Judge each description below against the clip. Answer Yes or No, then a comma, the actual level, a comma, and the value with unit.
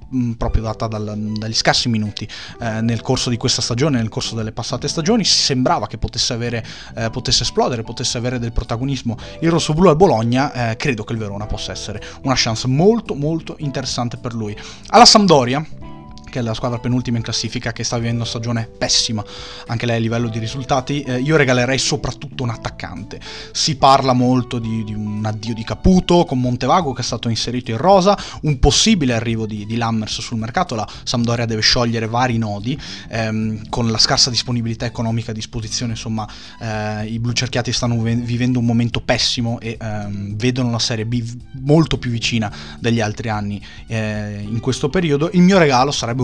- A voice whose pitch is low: Yes, low, 120 Hz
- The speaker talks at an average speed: No, fast, 185 wpm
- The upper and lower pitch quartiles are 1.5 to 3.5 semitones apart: Yes, narrow, 2.5 semitones